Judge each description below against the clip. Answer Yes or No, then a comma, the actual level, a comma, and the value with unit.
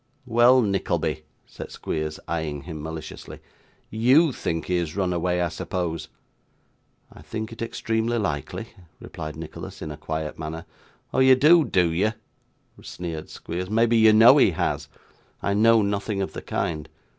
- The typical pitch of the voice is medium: No, very low, 90 Hz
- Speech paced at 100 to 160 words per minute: Yes, average, 155 wpm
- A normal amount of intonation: No, wide, 5.9 semitones